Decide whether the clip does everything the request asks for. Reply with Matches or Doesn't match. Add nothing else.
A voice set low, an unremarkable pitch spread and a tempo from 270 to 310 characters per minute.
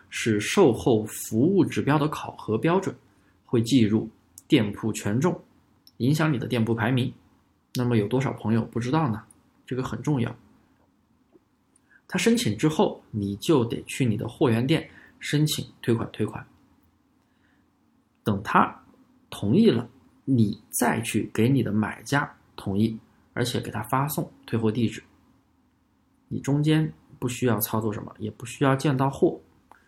Doesn't match